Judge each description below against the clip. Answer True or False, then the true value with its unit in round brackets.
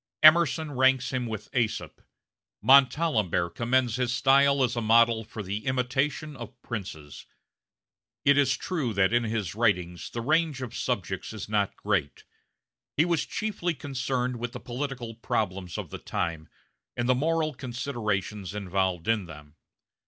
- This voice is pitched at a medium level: False (120 Hz)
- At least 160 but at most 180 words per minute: False (145 wpm)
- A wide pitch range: False (4.7 semitones)